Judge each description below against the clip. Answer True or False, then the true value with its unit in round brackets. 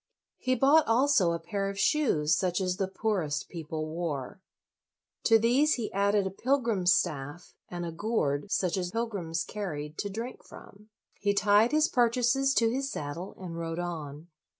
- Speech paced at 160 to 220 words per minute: True (165 wpm)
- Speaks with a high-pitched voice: True (195 Hz)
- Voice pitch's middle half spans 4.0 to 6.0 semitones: True (5.6 semitones)